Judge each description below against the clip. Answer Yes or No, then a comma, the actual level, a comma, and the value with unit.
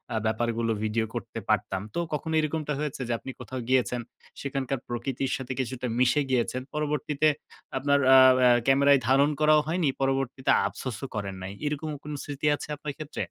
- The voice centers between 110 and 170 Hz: Yes, low, 135 Hz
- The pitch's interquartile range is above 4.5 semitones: No, average, 3.2 semitones